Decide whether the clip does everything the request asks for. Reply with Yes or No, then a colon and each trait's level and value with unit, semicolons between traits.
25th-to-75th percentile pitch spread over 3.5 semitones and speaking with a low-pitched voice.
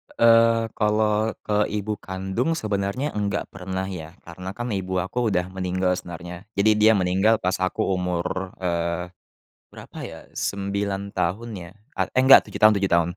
No: average, 2.9 semitones; very low, 95 Hz